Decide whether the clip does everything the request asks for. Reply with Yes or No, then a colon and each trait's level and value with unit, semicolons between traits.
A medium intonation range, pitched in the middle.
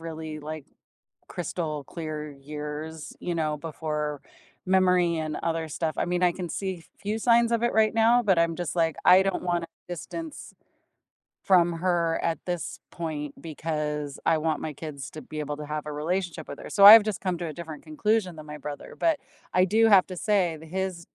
Yes: average, 3.3 semitones; medium, 165 Hz